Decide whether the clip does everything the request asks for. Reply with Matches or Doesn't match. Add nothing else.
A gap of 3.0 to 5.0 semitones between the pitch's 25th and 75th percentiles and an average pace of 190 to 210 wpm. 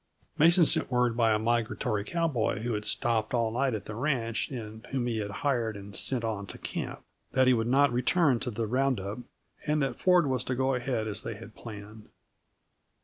Matches